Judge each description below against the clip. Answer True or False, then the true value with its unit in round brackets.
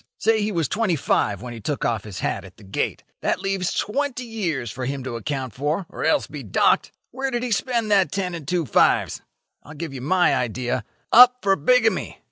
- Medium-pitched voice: True (170 Hz)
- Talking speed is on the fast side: True (215 wpm)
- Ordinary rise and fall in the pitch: False (8.9 semitones)